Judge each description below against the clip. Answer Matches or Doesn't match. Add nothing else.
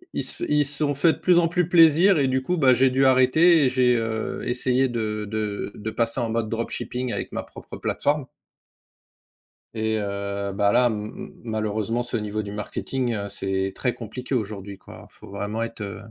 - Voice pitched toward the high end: Doesn't match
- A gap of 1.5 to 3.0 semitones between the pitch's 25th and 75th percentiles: Doesn't match